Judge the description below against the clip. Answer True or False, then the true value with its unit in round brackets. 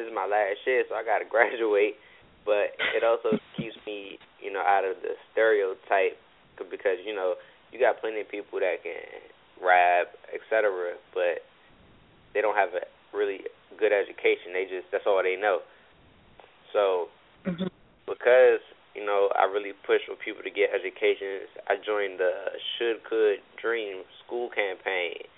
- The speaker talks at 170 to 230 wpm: False (155 wpm)